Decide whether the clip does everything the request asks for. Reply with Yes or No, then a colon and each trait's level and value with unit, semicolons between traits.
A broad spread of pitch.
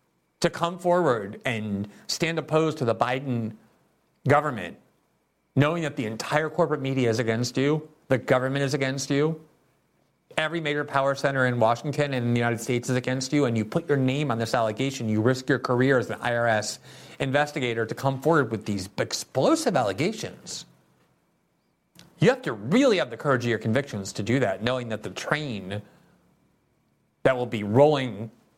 No: average, 4.1 semitones